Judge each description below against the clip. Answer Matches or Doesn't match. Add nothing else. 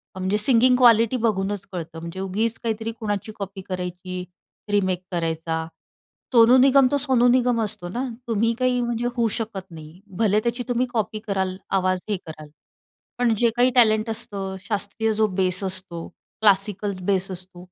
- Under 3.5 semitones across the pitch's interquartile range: Doesn't match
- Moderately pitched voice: Doesn't match